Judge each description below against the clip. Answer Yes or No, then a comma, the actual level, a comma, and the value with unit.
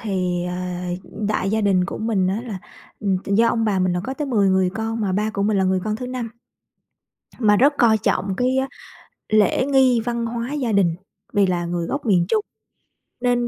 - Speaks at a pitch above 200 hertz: Yes, high, 215 Hz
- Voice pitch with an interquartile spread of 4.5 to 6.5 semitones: No, average, 3.8 semitones